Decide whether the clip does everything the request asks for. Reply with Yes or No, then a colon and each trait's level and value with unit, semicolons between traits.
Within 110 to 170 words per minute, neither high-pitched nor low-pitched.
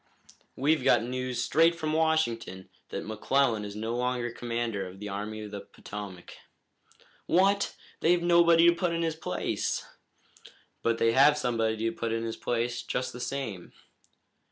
No: average, 155 wpm; low, 120 Hz